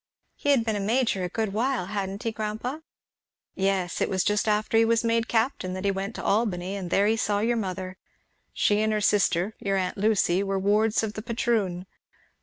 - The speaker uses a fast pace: Yes, fast, 210 wpm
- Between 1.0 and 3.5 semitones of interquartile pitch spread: Yes, narrow, 2.6 semitones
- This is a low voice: No, high, 210 Hz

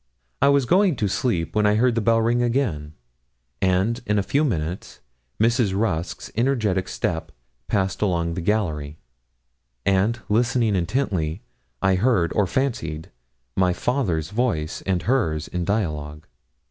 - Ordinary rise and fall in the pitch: No, wide, 5.8 semitones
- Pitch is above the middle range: No, low, 100 Hz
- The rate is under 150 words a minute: Yes, average, 140 wpm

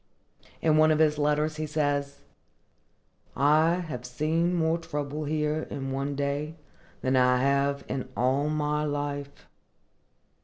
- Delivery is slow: Yes, slow, 130 wpm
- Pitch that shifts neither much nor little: No, narrow, 1.7 semitones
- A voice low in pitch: No, medium, 150 Hz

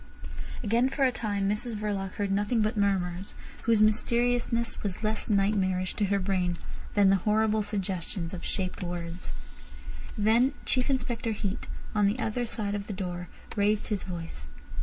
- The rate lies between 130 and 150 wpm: No, average, 160 wpm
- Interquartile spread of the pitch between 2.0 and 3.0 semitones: Yes, average, 2.7 semitones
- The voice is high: Yes, high, 205 Hz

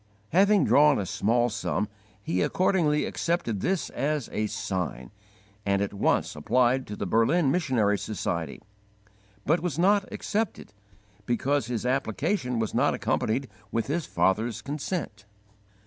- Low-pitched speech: Yes, low, 125 Hz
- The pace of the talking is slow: Yes, slow, 130 wpm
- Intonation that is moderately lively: No, wide, 6.6 semitones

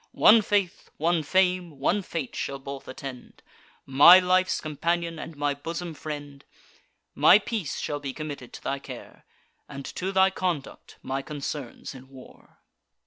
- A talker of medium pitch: Yes, medium, 155 Hz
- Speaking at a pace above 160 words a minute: No, average, 145 wpm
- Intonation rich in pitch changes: No, average, 4.7 semitones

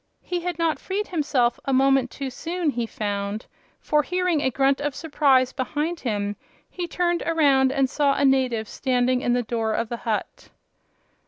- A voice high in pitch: Yes, very high, 270 Hz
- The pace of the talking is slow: No, average, 175 wpm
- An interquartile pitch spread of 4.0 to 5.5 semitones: Yes, average, 4.5 semitones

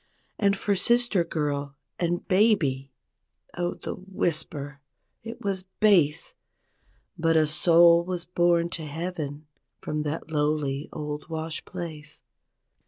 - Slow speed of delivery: Yes, slow, 115 wpm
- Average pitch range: Yes, average, 3.3 semitones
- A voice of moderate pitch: Yes, medium, 165 Hz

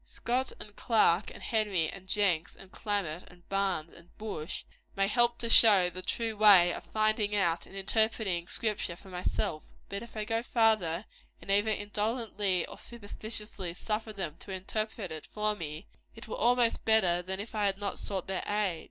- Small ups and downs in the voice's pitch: No, average, 3.2 semitones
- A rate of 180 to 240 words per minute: Yes, average, 185 wpm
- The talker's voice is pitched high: Yes, high, 205 Hz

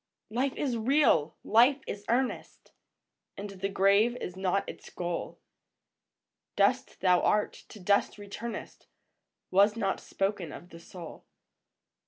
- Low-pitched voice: No, high, 200 Hz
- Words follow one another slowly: Yes, slow, 125 wpm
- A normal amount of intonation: Yes, average, 3.8 semitones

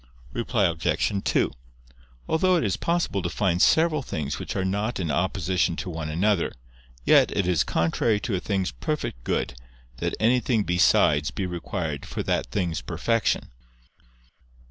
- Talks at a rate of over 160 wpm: No, average, 150 wpm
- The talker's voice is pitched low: Yes, very low, 95 Hz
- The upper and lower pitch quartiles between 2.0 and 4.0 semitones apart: No, average, 4.5 semitones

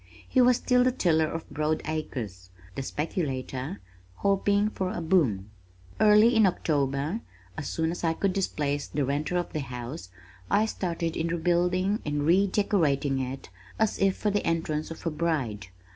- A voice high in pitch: No, medium, 165 Hz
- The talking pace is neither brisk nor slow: Yes, average, 160 wpm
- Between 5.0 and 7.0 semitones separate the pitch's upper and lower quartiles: Yes, average, 5.3 semitones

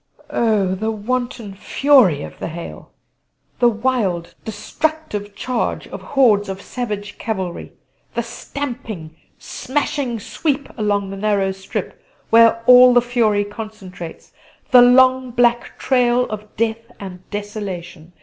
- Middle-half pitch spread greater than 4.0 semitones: No, average, 3.7 semitones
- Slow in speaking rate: Yes, slow, 120 wpm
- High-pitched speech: Yes, high, 220 Hz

